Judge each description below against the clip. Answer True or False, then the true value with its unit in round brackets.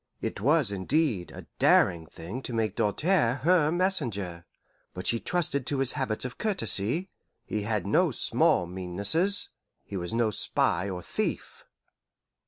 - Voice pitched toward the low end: True (115 Hz)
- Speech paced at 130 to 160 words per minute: True (145 wpm)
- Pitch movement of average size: False (8.0 semitones)